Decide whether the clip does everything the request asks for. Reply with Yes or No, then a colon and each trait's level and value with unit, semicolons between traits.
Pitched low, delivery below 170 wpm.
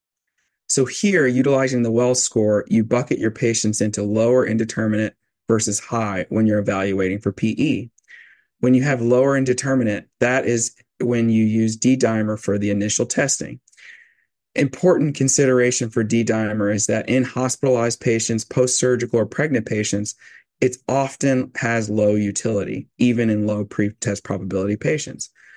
Yes: low, 115 Hz; average, 145 wpm